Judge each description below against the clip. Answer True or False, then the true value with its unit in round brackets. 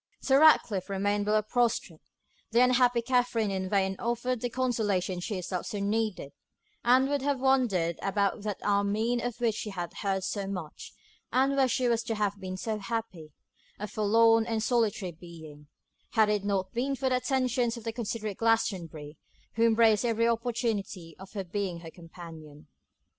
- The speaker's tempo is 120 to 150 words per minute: False (165 wpm)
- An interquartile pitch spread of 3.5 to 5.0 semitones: True (3.9 semitones)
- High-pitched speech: True (215 Hz)